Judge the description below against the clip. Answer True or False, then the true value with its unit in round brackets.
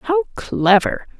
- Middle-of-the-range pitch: False (270 Hz)